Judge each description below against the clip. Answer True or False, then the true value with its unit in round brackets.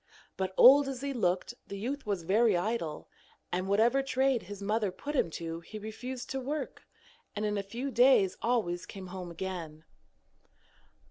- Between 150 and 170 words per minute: True (165 wpm)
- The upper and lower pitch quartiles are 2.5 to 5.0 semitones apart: False (5.4 semitones)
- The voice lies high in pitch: True (210 Hz)